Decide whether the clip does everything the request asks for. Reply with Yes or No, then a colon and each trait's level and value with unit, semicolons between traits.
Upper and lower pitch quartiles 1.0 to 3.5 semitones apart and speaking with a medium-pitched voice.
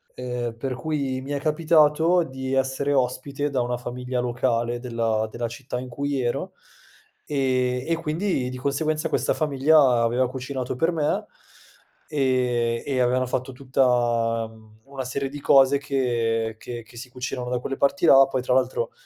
No: narrow, 2.4 semitones; low, 130 Hz